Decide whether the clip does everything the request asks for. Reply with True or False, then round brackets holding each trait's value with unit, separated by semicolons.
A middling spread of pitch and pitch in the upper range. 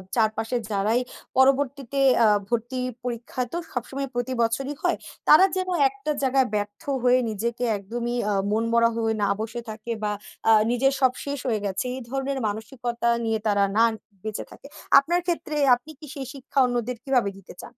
True (3.4 semitones; 245 Hz)